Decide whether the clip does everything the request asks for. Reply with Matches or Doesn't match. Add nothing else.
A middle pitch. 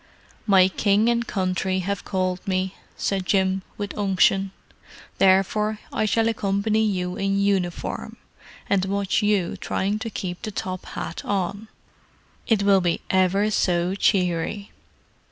Doesn't match